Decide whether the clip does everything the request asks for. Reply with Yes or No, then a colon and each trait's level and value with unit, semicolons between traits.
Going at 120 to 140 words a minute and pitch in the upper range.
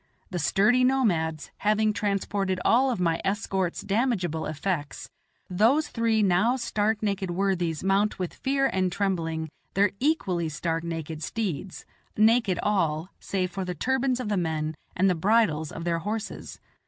No: average, 150 wpm; high, 195 Hz